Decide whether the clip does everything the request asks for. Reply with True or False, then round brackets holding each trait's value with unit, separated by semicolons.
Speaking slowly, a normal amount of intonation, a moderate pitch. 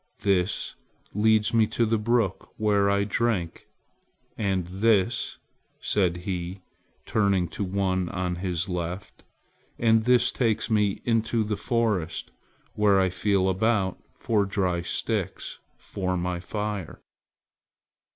False (120 wpm; 3.0 semitones; 100 Hz)